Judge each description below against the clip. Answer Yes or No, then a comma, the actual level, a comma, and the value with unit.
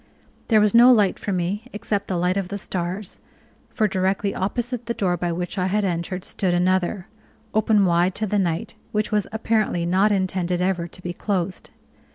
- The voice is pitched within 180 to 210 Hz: Yes, high, 190 Hz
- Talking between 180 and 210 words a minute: Yes, average, 190 wpm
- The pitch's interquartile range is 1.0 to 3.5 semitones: Yes, average, 2.8 semitones